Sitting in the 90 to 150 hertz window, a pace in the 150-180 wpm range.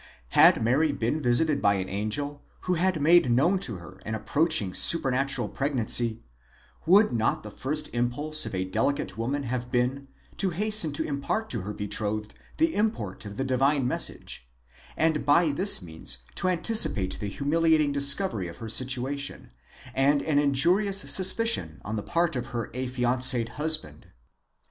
Yes: low, 135 Hz; average, 160 wpm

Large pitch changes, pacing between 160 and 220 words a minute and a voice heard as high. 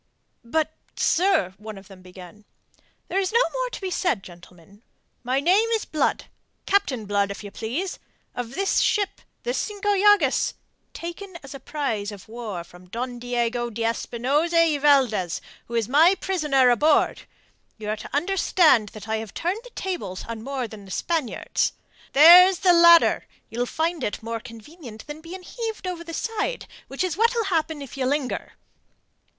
Yes: wide, 8.3 semitones; average, 170 wpm; very high, 275 Hz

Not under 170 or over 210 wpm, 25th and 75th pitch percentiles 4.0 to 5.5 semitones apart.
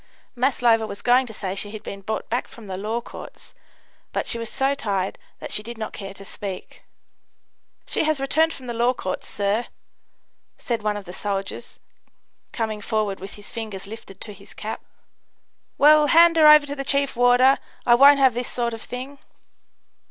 Yes: average, 190 wpm; average, 4.4 semitones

